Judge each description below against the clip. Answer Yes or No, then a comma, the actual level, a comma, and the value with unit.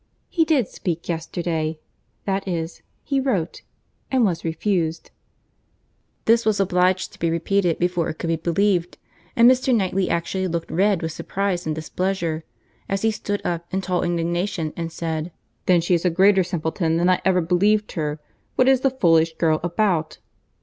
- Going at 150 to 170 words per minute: Yes, average, 165 wpm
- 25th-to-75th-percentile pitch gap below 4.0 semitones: Yes, average, 3.2 semitones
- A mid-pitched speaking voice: Yes, medium, 175 Hz